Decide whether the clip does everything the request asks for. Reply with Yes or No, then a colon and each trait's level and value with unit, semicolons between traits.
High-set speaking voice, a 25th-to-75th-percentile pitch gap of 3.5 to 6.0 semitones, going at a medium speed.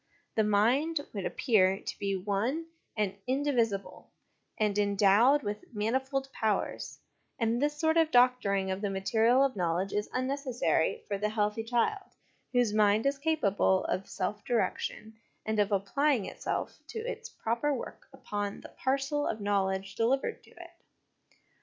Yes: high, 220 Hz; average, 5.1 semitones; average, 145 wpm